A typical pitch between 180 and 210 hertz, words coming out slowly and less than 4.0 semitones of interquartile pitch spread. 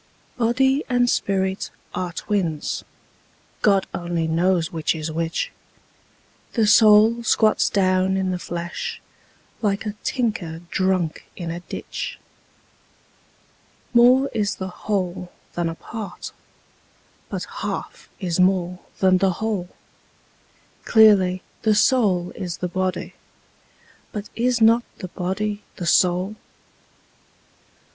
Yes: high, 190 Hz; slow, 110 wpm; average, 3.4 semitones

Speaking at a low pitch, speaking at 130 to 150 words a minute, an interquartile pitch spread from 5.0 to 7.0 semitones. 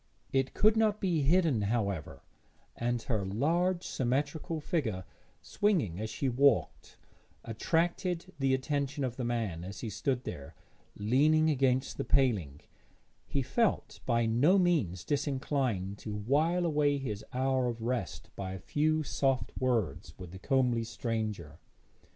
Yes: low, 130 Hz; average, 140 wpm; wide, 5.5 semitones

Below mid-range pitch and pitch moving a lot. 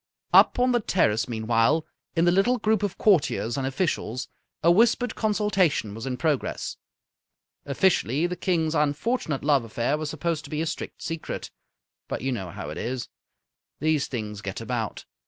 No: medium, 150 Hz; wide, 7.2 semitones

